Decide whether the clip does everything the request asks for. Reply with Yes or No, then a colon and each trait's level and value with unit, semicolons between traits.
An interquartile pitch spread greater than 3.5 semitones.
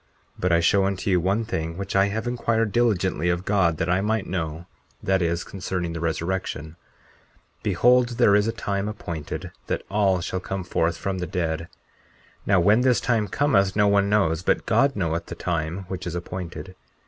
No: average, 3.2 semitones